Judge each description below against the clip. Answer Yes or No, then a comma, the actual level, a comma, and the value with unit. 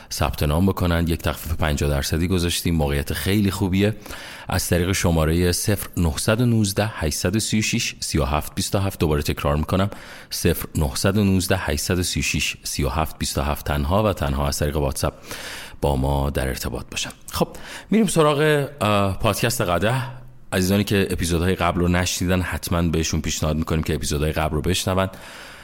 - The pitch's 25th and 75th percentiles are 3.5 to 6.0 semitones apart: Yes, average, 4.5 semitones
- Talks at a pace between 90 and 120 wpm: No, average, 130 wpm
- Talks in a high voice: No, very low, 90 Hz